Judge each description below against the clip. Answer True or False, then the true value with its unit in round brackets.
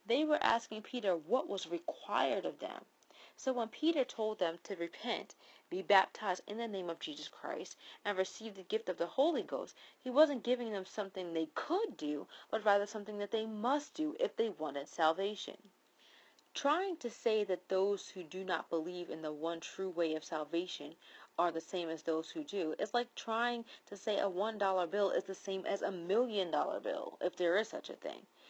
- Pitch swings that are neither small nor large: True (4.7 semitones)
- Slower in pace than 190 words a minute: False (200 wpm)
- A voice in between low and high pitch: False (200 Hz)